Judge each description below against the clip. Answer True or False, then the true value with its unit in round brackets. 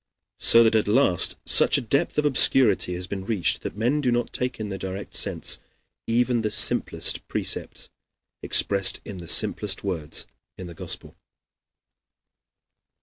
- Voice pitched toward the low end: True (105 Hz)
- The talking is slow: False (150 wpm)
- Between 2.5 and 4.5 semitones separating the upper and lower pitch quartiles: True (4.2 semitones)